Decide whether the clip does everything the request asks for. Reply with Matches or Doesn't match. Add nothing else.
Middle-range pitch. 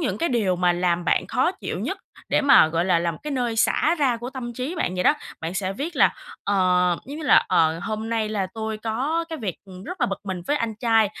Doesn't match